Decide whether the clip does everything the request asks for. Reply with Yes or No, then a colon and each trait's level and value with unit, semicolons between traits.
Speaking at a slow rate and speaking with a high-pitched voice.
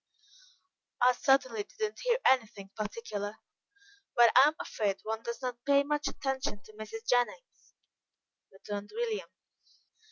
Yes: slow, 125 wpm; high, 240 Hz